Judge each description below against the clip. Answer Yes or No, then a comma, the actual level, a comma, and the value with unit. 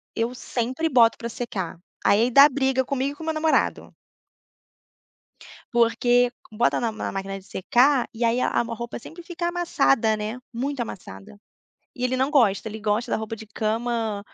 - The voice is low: No, high, 240 Hz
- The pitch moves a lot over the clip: No, average, 3.4 semitones